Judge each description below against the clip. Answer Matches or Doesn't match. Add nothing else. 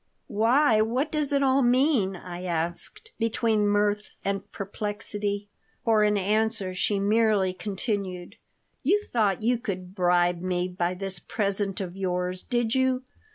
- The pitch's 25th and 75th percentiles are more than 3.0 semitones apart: Matches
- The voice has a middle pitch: Doesn't match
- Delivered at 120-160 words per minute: Matches